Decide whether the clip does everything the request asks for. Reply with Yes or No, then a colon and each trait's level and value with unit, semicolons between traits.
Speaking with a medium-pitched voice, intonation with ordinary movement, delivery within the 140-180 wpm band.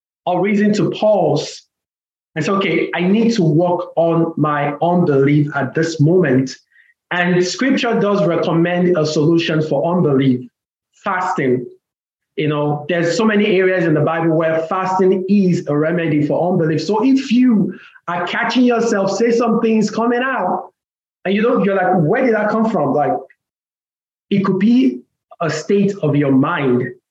Yes: medium, 175 Hz; average, 4.7 semitones; average, 160 wpm